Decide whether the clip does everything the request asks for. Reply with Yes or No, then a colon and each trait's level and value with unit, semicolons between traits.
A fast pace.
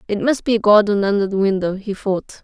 Yes: fast, 245 wpm